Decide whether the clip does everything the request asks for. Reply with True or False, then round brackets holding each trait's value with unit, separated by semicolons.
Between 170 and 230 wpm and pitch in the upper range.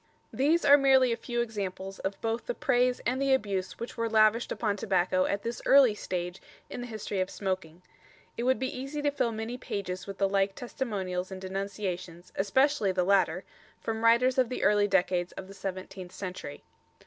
True (195 wpm; 205 Hz)